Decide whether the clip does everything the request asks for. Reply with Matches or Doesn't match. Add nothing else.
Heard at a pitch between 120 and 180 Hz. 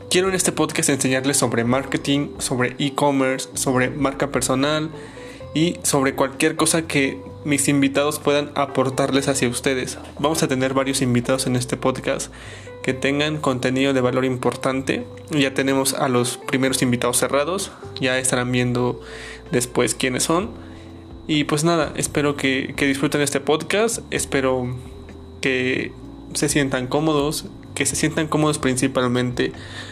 Matches